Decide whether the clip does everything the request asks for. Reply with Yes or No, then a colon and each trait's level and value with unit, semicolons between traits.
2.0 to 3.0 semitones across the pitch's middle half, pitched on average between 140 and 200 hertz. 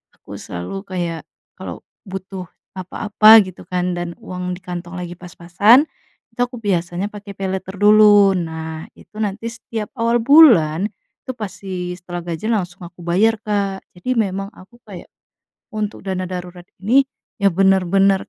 Yes: average, 2.7 semitones; high, 190 Hz